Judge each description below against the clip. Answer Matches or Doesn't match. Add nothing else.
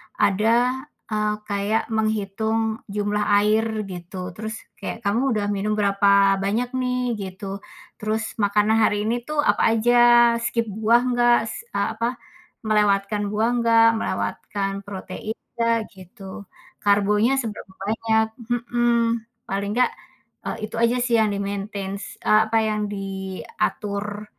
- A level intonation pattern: Matches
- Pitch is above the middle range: Matches